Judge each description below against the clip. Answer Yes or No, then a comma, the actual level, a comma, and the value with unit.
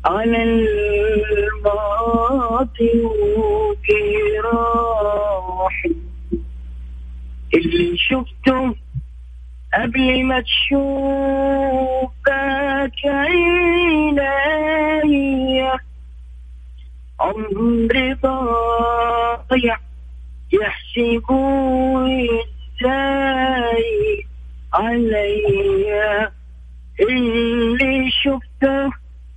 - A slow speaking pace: Yes, slow, 35 wpm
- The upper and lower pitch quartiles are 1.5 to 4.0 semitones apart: No, average, 5.2 semitones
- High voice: Yes, high, 235 Hz